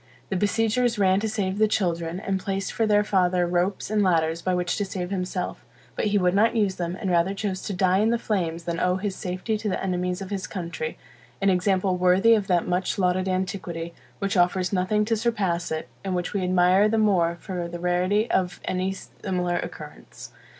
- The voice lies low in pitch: No, medium, 185 Hz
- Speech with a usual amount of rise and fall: No, narrow, 2.2 semitones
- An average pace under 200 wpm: No, fast, 205 wpm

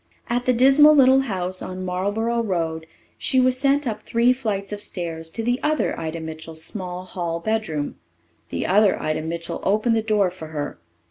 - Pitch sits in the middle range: No, high, 200 Hz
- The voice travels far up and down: Yes, wide, 6.1 semitones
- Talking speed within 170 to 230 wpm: Yes, average, 180 wpm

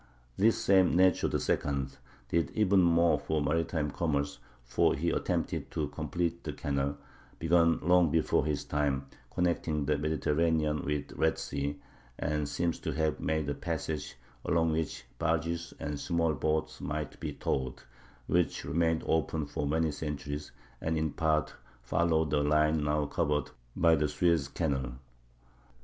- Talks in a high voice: No, very low, 80 Hz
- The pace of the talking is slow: No, average, 145 wpm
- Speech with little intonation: Yes, narrow, 2.3 semitones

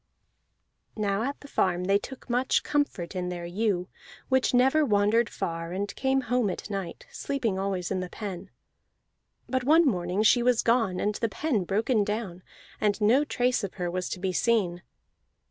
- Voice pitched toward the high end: Yes, high, 210 Hz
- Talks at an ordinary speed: Yes, average, 175 wpm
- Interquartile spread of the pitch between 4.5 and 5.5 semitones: Yes, average, 5.1 semitones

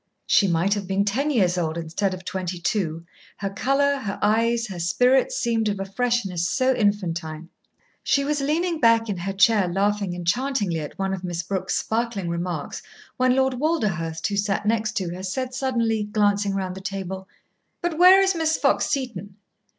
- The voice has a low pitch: No, high, 205 Hz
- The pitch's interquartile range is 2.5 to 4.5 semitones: No, average, 5.3 semitones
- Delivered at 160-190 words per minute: Yes, average, 180 wpm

